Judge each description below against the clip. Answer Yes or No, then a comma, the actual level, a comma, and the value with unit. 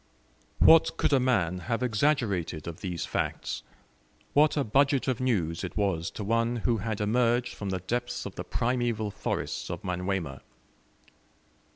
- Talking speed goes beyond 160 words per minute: No, average, 155 wpm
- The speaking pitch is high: No, low, 110 Hz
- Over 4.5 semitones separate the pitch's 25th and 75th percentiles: Yes, average, 5.0 semitones